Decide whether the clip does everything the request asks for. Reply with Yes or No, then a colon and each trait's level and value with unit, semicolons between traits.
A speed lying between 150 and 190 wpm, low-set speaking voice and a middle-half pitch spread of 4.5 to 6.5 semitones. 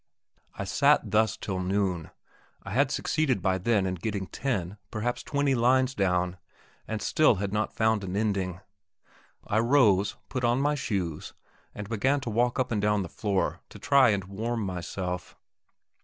No: average, 170 wpm; low, 105 Hz; average, 4.1 semitones